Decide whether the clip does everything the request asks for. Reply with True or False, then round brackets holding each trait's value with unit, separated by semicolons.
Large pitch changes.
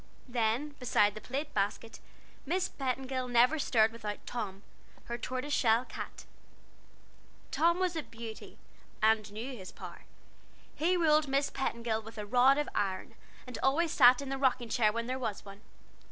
False (3.7 semitones)